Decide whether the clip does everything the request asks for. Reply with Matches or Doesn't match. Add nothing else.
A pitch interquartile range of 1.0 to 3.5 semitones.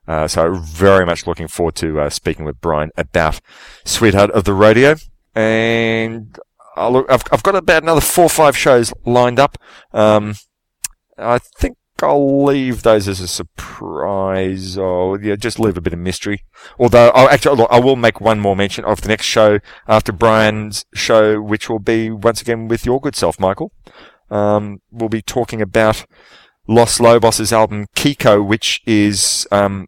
Matches